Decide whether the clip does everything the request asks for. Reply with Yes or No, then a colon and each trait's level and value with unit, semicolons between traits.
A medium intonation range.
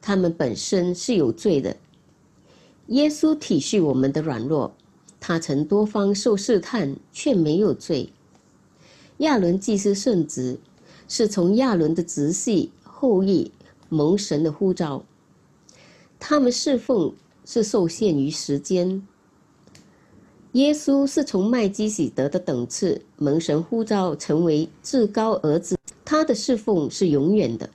No: wide, 7.2 semitones